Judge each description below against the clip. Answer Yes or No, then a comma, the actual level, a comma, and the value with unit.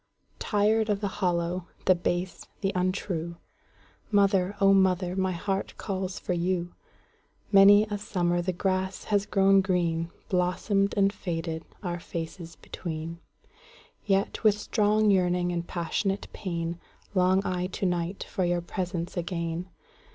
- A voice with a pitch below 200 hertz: Yes, medium, 185 Hz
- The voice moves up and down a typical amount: No, narrow, 2.2 semitones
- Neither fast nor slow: No, slow, 120 wpm